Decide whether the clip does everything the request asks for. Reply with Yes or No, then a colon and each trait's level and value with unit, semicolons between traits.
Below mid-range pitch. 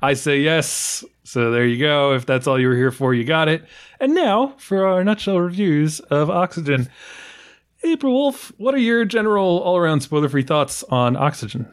No: medium, 155 Hz